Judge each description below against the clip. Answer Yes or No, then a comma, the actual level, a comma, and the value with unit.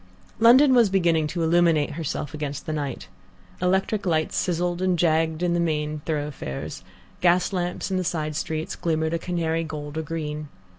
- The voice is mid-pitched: Yes, medium, 165 Hz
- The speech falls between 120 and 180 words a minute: Yes, average, 165 wpm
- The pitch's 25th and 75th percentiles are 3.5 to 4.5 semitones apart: No, narrow, 2.5 semitones